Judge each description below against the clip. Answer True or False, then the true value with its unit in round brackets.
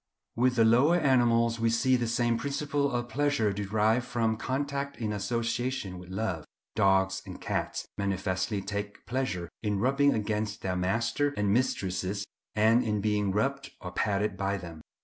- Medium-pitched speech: False (110 Hz)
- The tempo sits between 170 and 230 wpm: False (155 wpm)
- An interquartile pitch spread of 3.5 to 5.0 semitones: True (4.0 semitones)